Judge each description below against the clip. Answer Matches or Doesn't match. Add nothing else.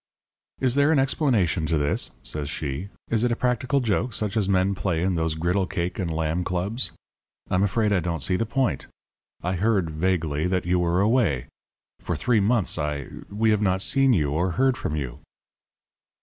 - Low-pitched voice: Matches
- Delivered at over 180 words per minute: Matches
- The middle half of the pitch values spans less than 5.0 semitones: Doesn't match